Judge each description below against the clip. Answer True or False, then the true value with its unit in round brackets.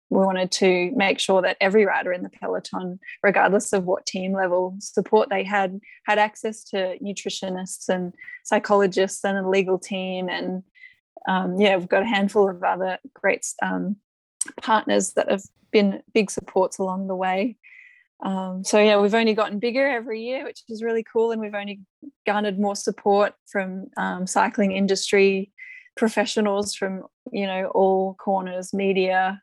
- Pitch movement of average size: False (2.3 semitones)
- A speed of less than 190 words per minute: True (160 wpm)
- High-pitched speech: True (200 Hz)